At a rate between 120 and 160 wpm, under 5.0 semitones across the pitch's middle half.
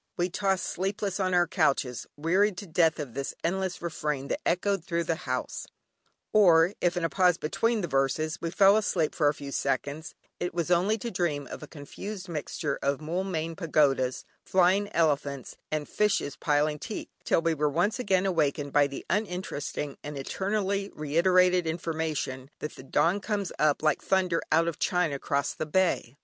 No: average, 175 wpm; average, 4.2 semitones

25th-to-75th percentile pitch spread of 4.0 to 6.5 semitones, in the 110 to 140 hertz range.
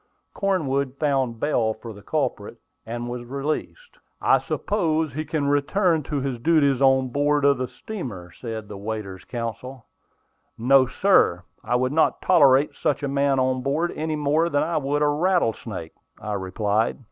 Yes: average, 4.3 semitones; low, 135 Hz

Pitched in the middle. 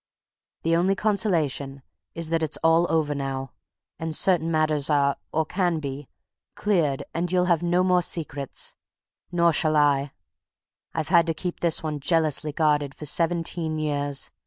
Yes: medium, 160 Hz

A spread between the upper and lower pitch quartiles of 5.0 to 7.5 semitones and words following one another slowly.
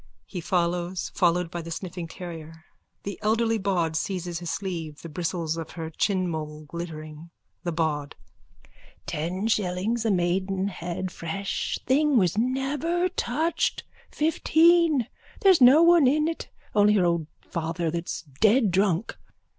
Yes: wide, 5.4 semitones; slow, 130 wpm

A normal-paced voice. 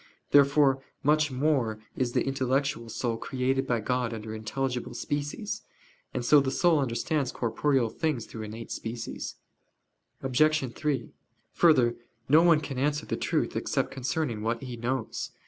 Yes: average, 145 wpm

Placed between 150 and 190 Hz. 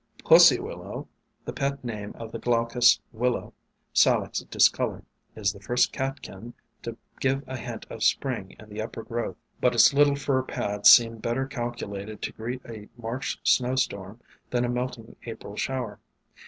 No: low, 120 Hz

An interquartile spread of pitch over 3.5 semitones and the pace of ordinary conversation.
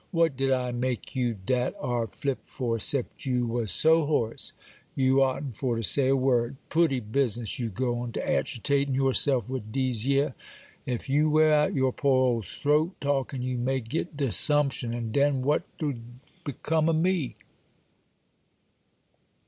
No: average, 2.8 semitones; average, 160 wpm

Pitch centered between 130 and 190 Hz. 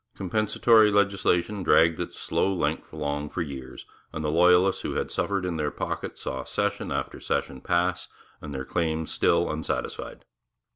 No: very low, 85 Hz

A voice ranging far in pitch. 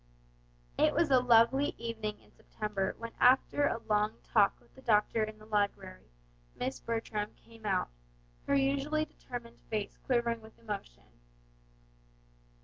No: average, 2.9 semitones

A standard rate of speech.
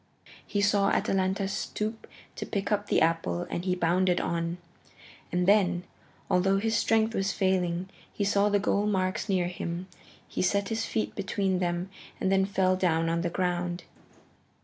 Yes: average, 165 wpm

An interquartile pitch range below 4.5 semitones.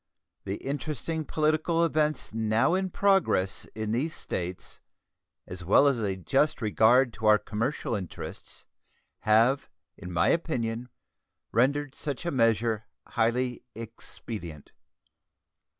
No: wide, 5.5 semitones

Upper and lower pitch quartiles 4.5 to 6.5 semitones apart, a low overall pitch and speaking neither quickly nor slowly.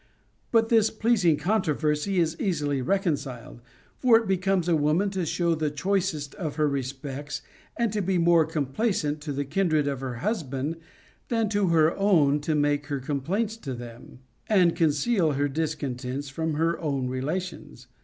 No: average, 5.1 semitones; medium, 155 Hz; average, 170 wpm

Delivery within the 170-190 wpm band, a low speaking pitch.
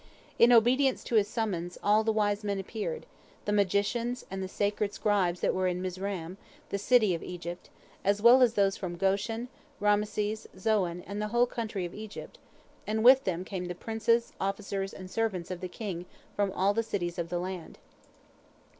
No: average, 180 wpm; high, 205 Hz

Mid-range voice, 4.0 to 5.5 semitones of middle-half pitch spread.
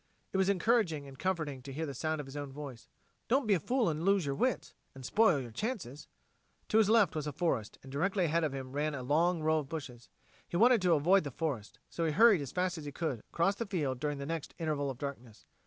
Yes: medium, 155 Hz; average, 5.1 semitones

